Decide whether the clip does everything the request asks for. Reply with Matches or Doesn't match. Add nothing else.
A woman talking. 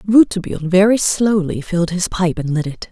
Matches